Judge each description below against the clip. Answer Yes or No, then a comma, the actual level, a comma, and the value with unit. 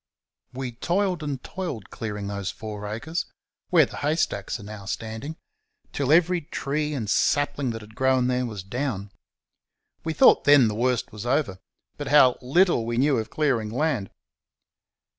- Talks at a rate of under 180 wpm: Yes, average, 160 wpm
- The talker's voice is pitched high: No, low, 125 Hz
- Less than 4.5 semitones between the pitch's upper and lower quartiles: No, wide, 5.4 semitones